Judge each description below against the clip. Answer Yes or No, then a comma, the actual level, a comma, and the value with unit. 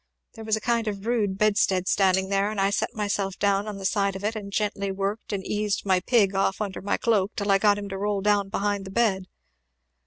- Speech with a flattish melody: Yes, narrow, 1.4 semitones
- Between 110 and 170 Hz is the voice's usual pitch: No, high, 200 Hz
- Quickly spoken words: Yes, fast, 245 wpm